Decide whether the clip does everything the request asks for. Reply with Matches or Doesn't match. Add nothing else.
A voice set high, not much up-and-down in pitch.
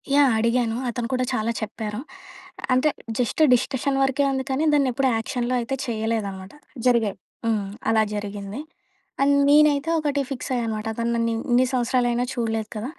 Doesn't match